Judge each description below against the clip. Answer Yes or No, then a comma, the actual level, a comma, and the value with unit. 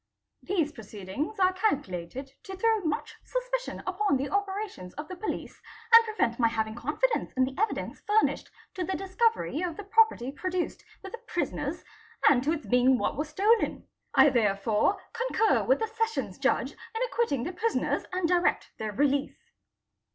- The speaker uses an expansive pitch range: Yes, wide, 8.7 semitones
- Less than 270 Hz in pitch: No, very high, 360 Hz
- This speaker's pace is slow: No, average, 165 wpm